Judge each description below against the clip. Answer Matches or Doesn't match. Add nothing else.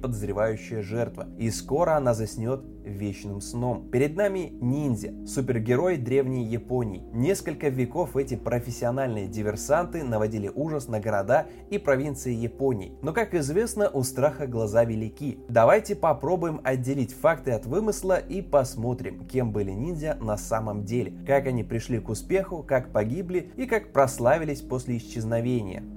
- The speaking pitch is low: Matches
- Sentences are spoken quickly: Doesn't match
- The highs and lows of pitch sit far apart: Doesn't match